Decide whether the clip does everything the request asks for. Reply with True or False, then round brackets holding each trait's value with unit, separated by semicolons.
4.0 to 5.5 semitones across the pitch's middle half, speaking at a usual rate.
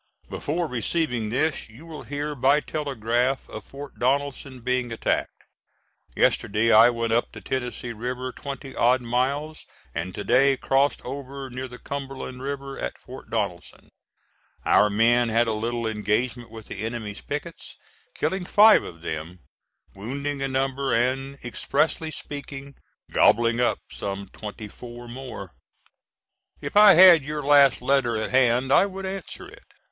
False (3.4 semitones; 145 wpm)